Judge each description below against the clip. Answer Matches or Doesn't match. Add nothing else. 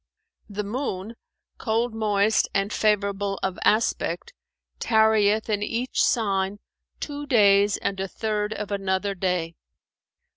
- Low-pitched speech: Doesn't match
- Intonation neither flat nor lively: Doesn't match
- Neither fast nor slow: Doesn't match